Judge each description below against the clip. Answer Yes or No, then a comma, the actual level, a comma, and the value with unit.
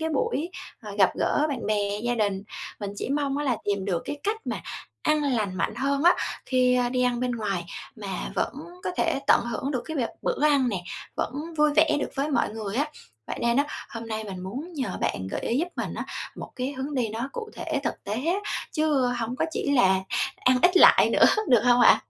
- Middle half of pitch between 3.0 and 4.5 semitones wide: No, average, 5.1 semitones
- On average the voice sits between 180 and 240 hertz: No, very high, 255 Hz